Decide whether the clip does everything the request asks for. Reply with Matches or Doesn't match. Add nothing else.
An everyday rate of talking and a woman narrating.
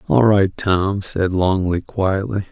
Doesn't match